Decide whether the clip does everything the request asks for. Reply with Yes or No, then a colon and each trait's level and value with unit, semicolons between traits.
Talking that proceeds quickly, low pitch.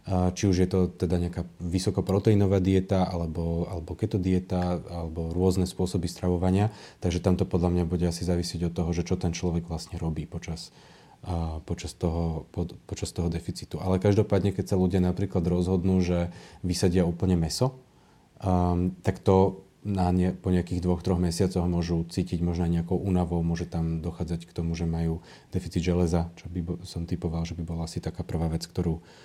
Yes: fast, 175 wpm; very low, 90 Hz